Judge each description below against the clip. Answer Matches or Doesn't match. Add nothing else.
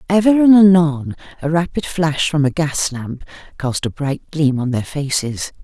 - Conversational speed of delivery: Matches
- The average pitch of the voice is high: Doesn't match